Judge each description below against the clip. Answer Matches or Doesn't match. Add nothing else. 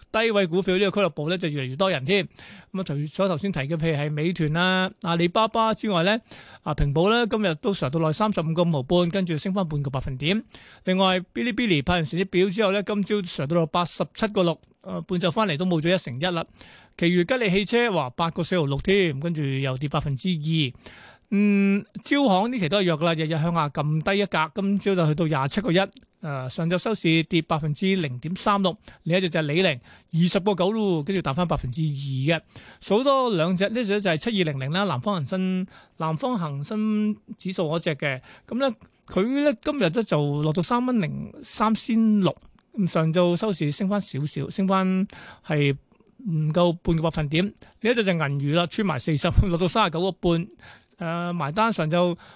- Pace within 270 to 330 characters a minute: Matches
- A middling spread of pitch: Matches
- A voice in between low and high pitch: Matches